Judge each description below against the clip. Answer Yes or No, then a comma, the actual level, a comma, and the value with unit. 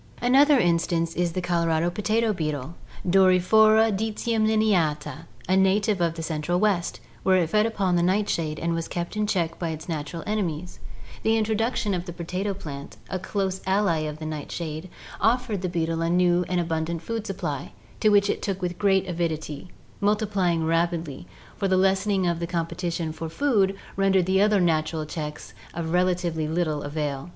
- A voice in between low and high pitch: Yes, medium, 175 Hz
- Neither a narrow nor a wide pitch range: Yes, average, 3.4 semitones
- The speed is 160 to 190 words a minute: Yes, average, 180 wpm